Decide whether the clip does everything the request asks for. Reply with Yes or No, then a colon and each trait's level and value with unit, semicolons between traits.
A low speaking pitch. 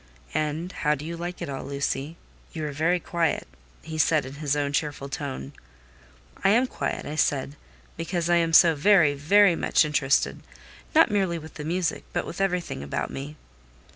No: medium, 155 Hz